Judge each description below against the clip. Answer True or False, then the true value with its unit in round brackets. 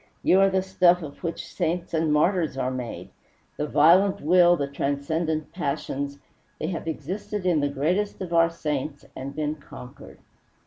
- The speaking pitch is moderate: True (160 Hz)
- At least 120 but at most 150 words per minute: False (165 wpm)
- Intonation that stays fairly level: False (3.8 semitones)